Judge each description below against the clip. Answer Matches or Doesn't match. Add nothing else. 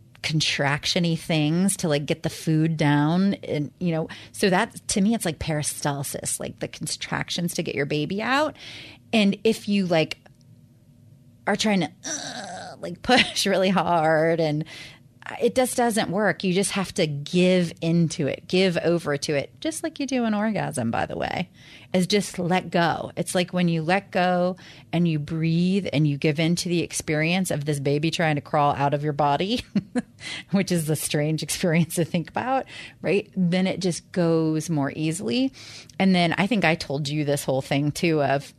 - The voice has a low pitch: Doesn't match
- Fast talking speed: Doesn't match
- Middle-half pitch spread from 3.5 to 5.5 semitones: Matches